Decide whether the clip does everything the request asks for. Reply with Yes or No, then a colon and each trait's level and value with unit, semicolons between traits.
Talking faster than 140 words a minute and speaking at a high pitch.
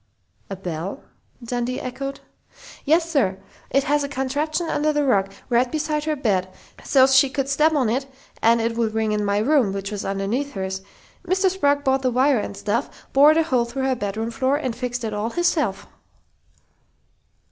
Yes: average, 180 wpm; very high, 255 Hz